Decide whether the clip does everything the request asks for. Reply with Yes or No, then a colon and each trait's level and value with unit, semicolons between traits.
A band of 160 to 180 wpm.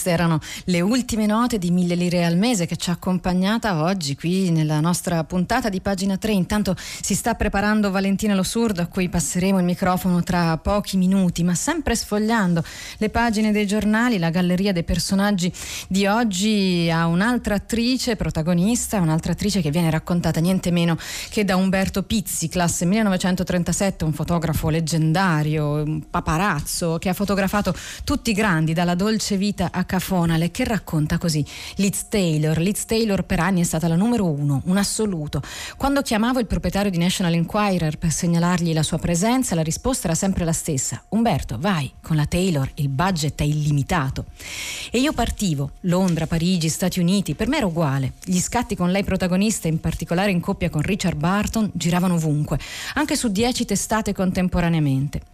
Yes: average, 165 wpm